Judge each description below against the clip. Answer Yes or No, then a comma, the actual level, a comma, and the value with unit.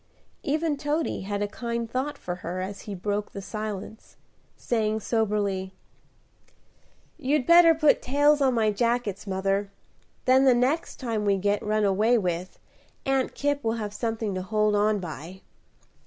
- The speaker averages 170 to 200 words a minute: No, average, 155 wpm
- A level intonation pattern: No, average, 4.4 semitones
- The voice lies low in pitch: No, high, 215 Hz